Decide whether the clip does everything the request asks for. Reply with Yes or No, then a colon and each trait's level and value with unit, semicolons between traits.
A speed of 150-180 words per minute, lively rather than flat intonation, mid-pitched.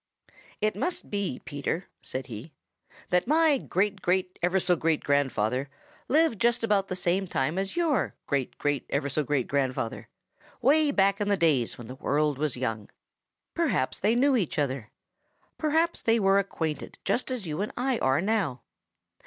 Yes: average, 170 wpm; wide, 8.0 semitones; medium, 180 Hz